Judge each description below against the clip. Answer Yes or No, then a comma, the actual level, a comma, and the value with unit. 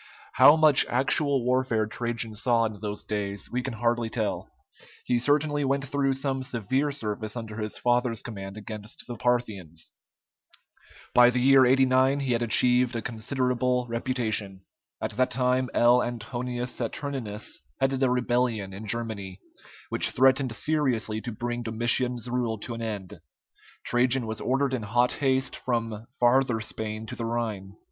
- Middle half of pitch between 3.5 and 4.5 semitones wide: No, average, 2.8 semitones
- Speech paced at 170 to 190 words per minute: No, average, 150 wpm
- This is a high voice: No, low, 120 Hz